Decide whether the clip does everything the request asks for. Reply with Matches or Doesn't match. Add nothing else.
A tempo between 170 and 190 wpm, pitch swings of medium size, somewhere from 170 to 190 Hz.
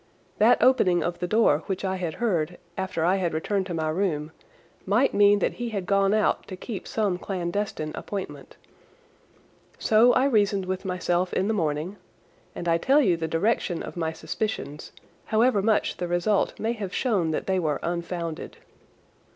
Matches